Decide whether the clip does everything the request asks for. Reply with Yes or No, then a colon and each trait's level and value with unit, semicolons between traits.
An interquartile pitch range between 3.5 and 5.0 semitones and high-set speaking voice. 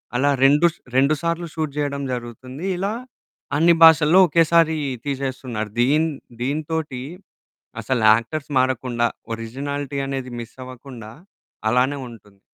No: average, 3.8 semitones; medium, 140 Hz